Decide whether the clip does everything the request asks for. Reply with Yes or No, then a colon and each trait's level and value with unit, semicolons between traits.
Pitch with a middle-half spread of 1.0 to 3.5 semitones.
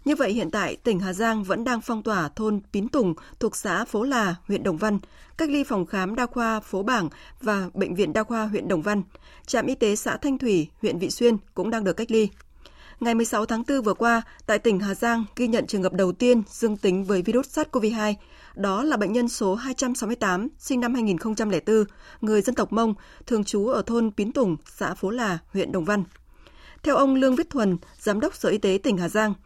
Yes: average, 3.2 semitones